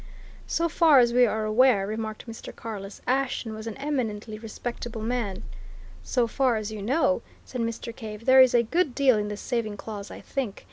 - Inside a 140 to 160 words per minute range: No, average, 190 wpm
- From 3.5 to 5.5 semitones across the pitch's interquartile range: No, average, 3.1 semitones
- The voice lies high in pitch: Yes, high, 230 Hz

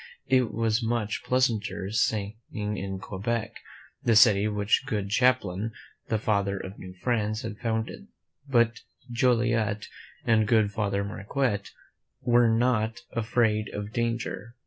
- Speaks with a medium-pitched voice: No, low, 110 Hz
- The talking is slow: Yes, slow, 125 wpm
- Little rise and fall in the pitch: Yes, narrow, 2.3 semitones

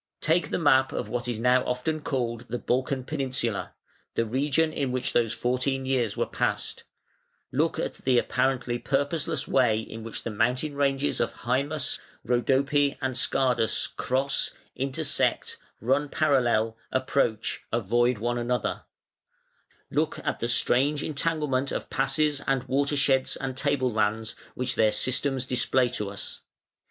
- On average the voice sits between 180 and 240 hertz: No, low, 130 Hz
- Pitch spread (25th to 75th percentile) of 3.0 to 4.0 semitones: No, narrow, 2.5 semitones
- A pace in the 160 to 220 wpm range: No, average, 145 wpm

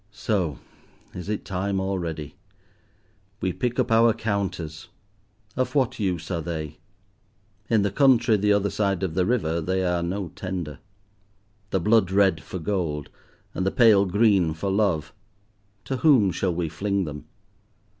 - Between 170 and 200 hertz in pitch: No, very low, 95 Hz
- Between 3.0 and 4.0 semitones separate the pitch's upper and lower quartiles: Yes, average, 3.7 semitones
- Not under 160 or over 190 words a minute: No, average, 150 wpm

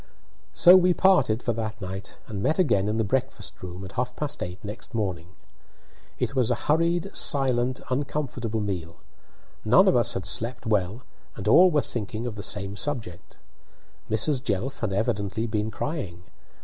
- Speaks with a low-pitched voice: Yes, low, 115 Hz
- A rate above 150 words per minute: Yes, average, 165 wpm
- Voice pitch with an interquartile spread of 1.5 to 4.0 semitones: No, wide, 5.4 semitones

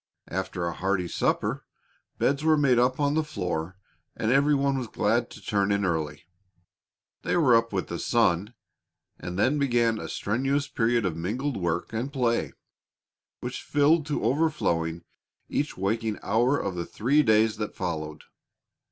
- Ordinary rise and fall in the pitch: No, wide, 6.8 semitones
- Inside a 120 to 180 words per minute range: Yes, average, 160 wpm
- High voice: No, low, 115 Hz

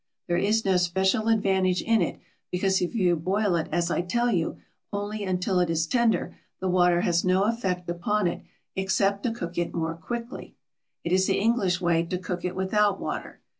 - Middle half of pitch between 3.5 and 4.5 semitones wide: No, average, 2.9 semitones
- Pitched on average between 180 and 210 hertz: Yes, medium, 185 Hz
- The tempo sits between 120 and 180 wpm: No, average, 195 wpm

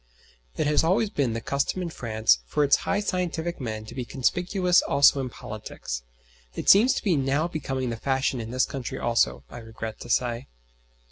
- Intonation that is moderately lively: No, wide, 6.4 semitones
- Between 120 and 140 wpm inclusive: No, average, 190 wpm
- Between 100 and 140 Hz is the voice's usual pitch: Yes, low, 135 Hz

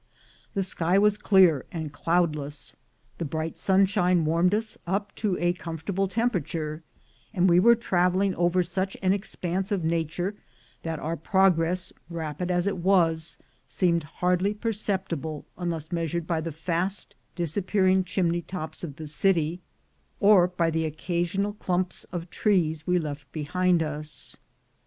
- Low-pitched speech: No, medium, 175 Hz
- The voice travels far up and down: No, average, 2.7 semitones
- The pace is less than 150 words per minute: Yes, average, 140 wpm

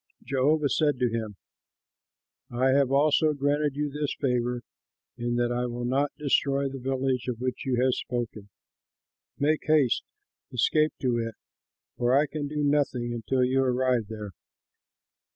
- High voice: No, low, 130 Hz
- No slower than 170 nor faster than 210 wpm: No, average, 150 wpm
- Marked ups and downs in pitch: No, average, 2.9 semitones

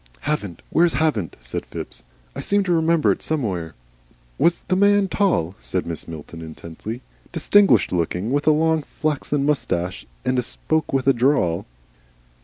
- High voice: No, low, 135 Hz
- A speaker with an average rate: Yes, average, 150 wpm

